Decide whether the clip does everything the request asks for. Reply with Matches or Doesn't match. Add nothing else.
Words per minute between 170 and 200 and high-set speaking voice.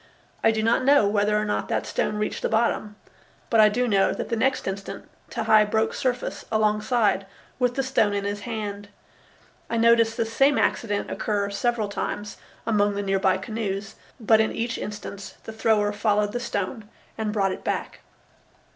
Matches